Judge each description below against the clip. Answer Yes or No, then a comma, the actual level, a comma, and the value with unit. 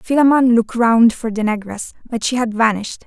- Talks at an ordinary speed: Yes, average, 195 wpm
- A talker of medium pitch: No, high, 230 Hz